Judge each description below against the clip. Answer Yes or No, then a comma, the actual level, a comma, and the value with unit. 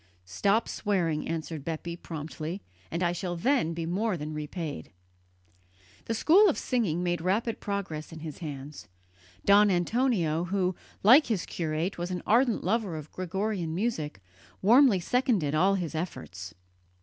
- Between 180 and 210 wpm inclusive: No, average, 145 wpm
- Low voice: No, medium, 175 Hz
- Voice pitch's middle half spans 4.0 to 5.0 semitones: Yes, average, 4.6 semitones